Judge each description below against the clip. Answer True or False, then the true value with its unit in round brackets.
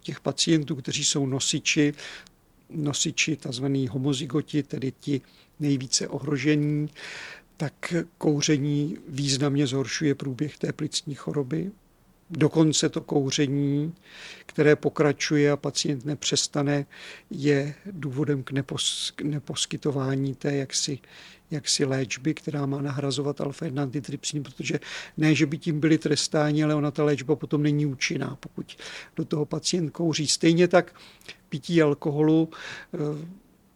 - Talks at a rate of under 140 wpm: True (115 wpm)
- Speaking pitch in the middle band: True (150 Hz)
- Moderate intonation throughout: False (1.7 semitones)